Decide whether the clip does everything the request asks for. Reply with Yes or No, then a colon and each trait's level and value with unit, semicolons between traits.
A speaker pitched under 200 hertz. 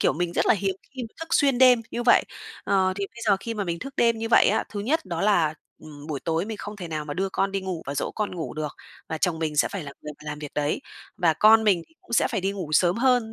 Yes: high, 190 Hz